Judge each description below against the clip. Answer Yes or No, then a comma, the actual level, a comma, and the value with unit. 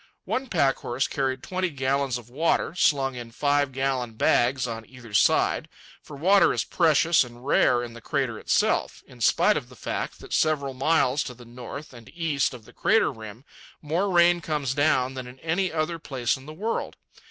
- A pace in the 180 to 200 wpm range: Yes, average, 185 wpm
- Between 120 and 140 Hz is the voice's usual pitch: Yes, low, 135 Hz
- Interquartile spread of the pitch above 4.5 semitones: No, average, 4.2 semitones